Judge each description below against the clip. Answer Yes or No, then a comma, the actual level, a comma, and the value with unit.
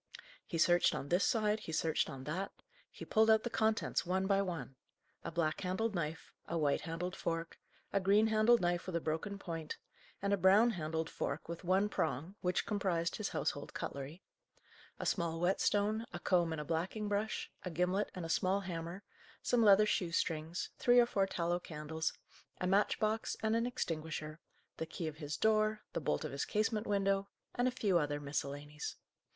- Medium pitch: Yes, medium, 180 Hz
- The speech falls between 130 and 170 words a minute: No, average, 190 wpm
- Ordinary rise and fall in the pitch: Yes, average, 4.3 semitones